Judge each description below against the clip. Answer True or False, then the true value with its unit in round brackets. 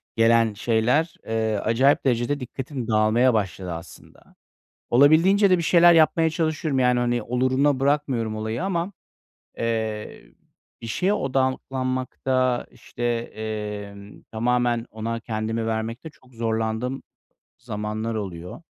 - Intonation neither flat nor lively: True (3.4 semitones)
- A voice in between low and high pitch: False (120 Hz)